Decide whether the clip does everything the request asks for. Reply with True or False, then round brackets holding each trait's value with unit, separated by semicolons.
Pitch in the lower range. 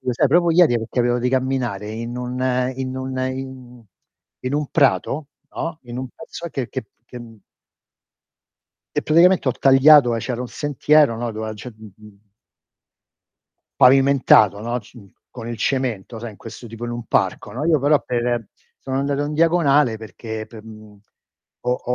True (125 Hz)